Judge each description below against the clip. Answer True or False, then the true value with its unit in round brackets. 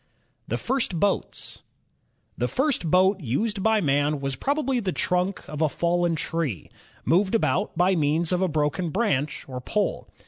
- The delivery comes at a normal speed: True (160 wpm)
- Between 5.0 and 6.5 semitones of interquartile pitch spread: True (5.3 semitones)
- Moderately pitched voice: True (175 Hz)